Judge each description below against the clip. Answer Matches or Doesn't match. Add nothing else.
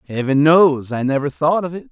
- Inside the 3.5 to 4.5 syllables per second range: Doesn't match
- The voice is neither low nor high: Matches